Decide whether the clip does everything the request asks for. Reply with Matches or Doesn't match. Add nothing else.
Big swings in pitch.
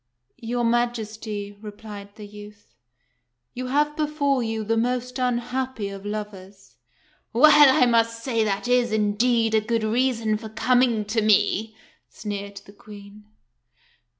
Doesn't match